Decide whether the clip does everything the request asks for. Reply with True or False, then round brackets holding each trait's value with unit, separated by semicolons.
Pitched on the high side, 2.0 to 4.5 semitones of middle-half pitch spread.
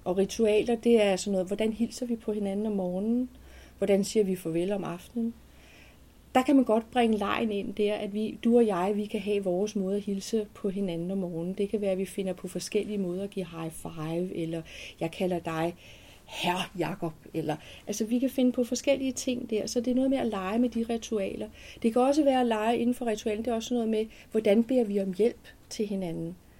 True (210 Hz; 3.8 semitones)